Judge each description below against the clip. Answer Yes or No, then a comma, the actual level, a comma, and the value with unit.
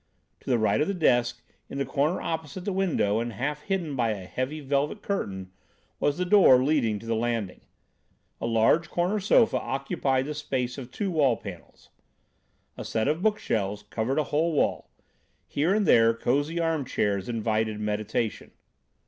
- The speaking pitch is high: No, low, 135 Hz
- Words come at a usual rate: Yes, average, 170 wpm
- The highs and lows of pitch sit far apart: Yes, wide, 5.9 semitones